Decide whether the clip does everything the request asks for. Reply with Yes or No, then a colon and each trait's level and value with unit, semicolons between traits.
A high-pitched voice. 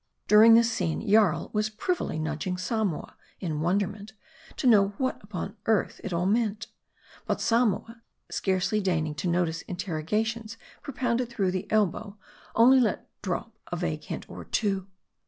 Yes: high, 205 Hz